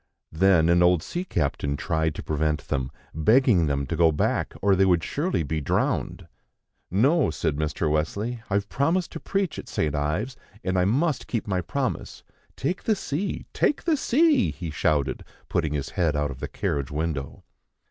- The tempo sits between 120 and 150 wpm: No, average, 180 wpm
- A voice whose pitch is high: No, very low, 90 Hz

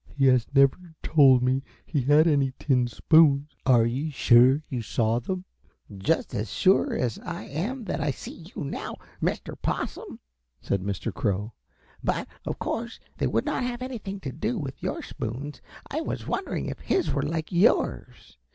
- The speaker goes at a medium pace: Yes, average, 170 wpm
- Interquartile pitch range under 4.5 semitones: No, wide, 5.4 semitones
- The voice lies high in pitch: No, medium, 140 Hz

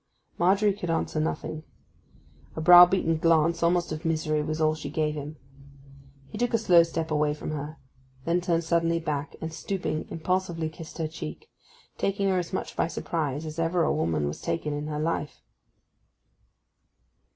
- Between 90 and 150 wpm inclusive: No, average, 165 wpm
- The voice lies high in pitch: No, medium, 160 Hz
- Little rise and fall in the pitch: Yes, narrow, 2.0 semitones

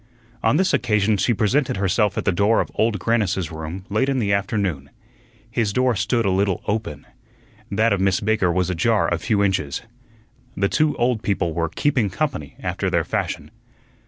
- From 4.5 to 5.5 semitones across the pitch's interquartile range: No, average, 3.7 semitones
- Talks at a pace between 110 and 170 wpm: No, average, 180 wpm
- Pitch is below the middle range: Yes, low, 100 Hz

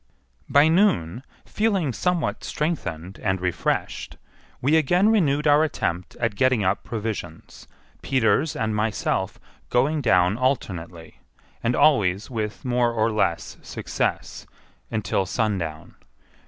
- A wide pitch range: Yes, wide, 7.4 semitones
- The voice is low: Yes, low, 115 Hz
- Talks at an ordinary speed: No, slow, 115 wpm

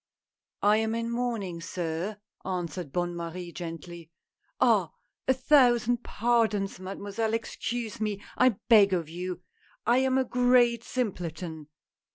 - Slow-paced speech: Yes, slow, 130 wpm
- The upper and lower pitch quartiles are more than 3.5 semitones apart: Yes, average, 5.2 semitones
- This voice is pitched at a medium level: No, high, 205 Hz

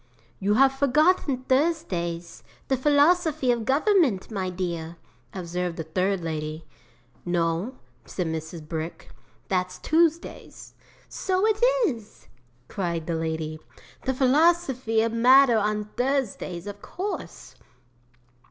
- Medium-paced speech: No, slow, 110 wpm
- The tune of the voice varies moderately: No, wide, 8.3 semitones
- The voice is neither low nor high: No, high, 215 Hz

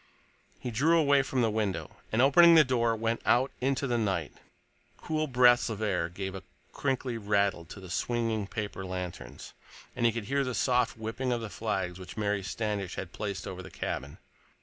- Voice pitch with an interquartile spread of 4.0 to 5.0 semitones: Yes, average, 4.4 semitones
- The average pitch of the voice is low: Yes, low, 110 Hz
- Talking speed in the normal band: Yes, average, 190 wpm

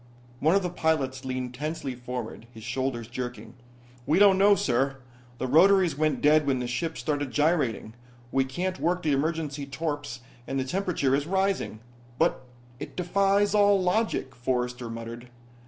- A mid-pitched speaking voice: Yes, medium, 145 Hz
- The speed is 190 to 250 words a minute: No, average, 155 wpm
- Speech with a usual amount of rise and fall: No, wide, 5.8 semitones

